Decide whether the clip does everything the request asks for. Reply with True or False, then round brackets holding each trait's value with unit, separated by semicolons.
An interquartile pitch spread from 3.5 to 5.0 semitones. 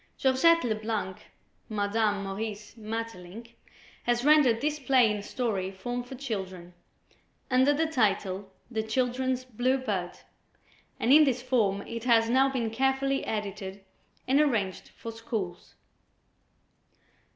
True (4.2 semitones)